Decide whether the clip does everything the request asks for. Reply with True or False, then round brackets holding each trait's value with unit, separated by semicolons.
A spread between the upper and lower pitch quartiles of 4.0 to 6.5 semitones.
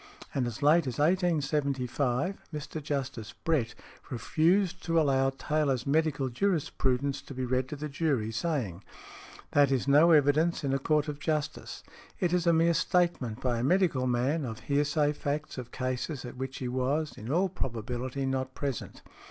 False (3.5 semitones)